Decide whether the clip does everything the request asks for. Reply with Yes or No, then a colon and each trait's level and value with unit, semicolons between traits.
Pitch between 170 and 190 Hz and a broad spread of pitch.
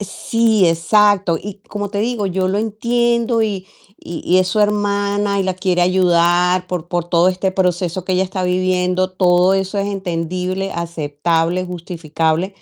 No: medium, 185 Hz; narrow, 2.4 semitones